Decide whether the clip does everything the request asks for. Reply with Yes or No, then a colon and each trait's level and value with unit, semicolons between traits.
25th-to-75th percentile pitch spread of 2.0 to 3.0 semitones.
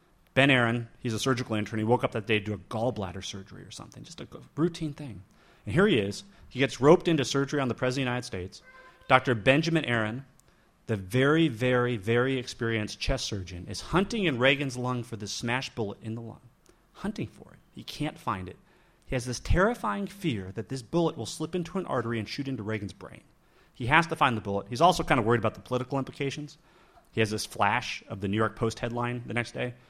No: average, 4.1 semitones